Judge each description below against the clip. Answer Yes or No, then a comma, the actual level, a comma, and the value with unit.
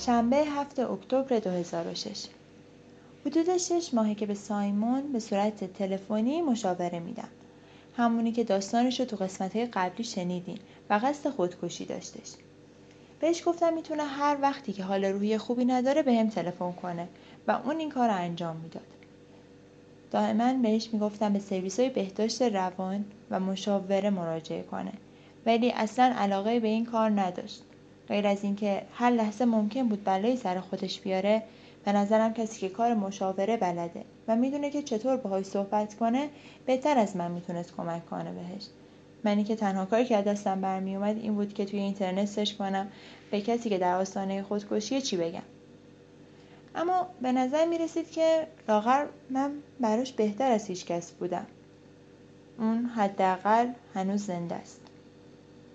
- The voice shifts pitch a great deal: No, average, 4.2 semitones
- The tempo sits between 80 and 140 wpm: No, average, 150 wpm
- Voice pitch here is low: No, high, 210 Hz